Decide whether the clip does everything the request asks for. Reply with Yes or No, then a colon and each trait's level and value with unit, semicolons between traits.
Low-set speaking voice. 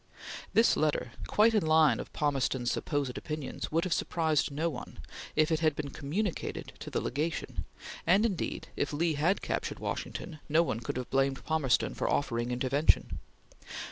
No: medium, 155 Hz